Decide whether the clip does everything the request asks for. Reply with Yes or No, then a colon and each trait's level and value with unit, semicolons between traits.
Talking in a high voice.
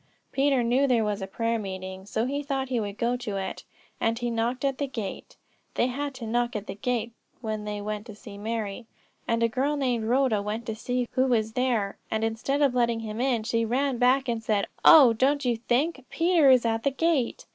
Yes: high, 235 Hz